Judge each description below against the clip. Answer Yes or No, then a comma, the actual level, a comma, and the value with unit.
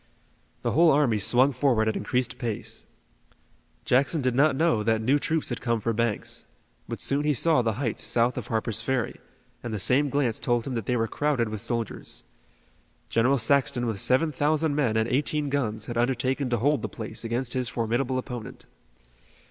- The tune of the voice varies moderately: Yes, average, 3.5 semitones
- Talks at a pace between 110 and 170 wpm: No, average, 185 wpm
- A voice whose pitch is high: No, low, 125 Hz